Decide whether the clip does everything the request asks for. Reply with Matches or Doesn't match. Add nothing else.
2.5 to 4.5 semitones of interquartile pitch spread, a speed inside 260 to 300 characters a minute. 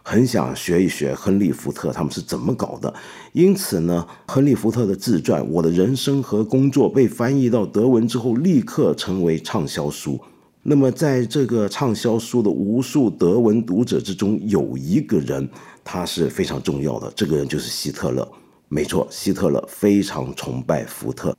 Doesn't match